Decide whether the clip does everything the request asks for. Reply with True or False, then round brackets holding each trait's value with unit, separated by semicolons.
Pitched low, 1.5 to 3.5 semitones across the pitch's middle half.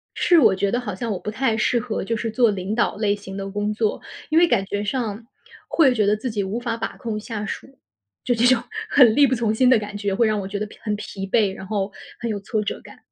False (215 Hz; 2.8 semitones)